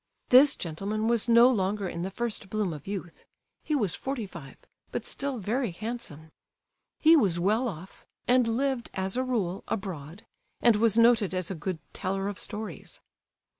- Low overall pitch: No, high, 210 Hz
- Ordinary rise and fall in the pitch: Yes, average, 4.3 semitones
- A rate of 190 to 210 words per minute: No, average, 165 wpm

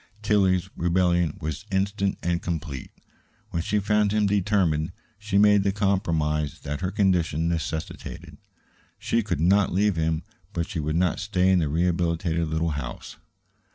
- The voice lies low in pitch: Yes, very low, 90 Hz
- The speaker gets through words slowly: No, average, 150 wpm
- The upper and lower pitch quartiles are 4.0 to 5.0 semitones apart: No, average, 3.5 semitones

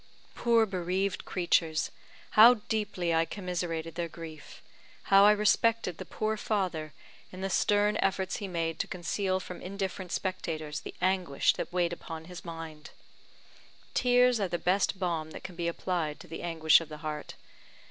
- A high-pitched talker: No, medium, 180 Hz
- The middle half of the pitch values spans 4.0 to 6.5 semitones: No, average, 3.2 semitones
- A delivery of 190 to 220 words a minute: No, average, 160 wpm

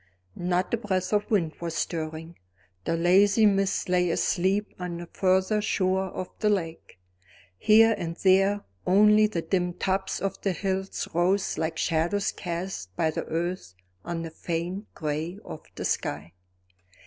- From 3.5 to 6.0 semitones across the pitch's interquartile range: No, average, 2.8 semitones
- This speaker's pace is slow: No, average, 150 wpm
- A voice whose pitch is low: No, medium, 185 Hz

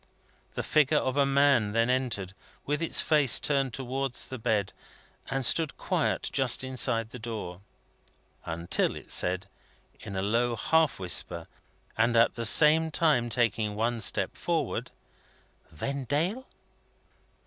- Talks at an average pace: No, slow, 130 wpm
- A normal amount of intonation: Yes, average, 4.1 semitones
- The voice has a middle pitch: No, low, 125 Hz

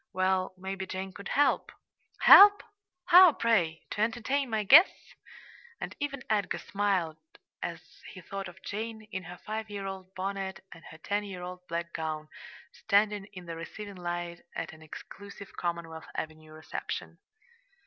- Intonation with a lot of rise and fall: No, average, 3.6 semitones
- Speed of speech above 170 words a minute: No, average, 150 wpm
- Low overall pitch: No, high, 190 Hz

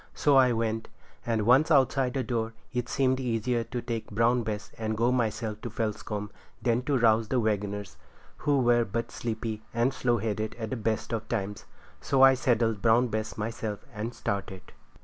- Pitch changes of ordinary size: No, narrow, 2.2 semitones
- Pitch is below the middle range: Yes, low, 115 Hz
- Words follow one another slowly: No, average, 180 wpm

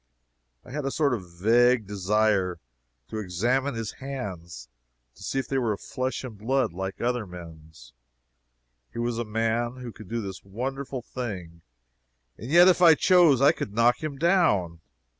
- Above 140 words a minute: Yes, average, 170 wpm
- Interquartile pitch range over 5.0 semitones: Yes, wide, 5.6 semitones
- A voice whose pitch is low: Yes, low, 115 Hz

